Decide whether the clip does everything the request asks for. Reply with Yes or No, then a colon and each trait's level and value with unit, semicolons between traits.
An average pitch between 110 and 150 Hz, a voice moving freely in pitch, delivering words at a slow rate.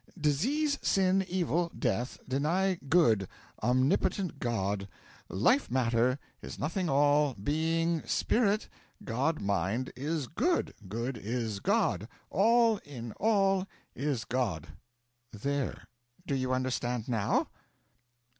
Yes: medium, 140 Hz; wide, 7.4 semitones; slow, 105 wpm